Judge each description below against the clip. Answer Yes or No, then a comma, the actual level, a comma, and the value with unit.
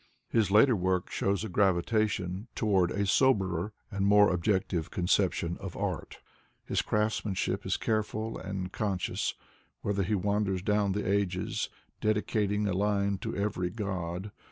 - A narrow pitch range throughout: Yes, narrow, 2.2 semitones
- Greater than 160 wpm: No, average, 140 wpm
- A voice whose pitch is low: Yes, low, 100 Hz